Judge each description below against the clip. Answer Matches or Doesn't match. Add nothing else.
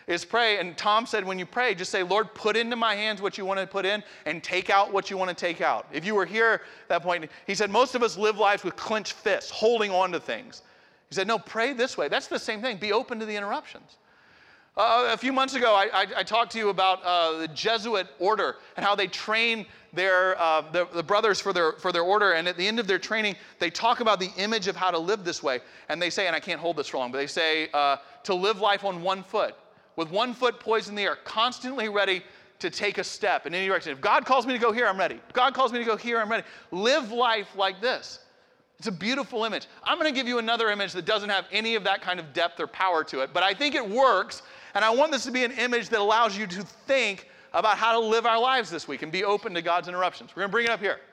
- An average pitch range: Matches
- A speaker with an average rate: Doesn't match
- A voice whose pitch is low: Doesn't match